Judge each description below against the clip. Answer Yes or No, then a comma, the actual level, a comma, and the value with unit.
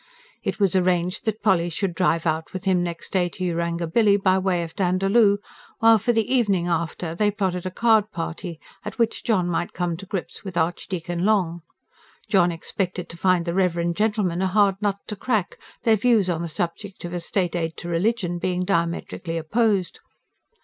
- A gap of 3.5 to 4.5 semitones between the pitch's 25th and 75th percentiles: No, average, 3.0 semitones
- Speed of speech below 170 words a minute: No, average, 185 wpm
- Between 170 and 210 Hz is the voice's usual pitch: Yes, medium, 185 Hz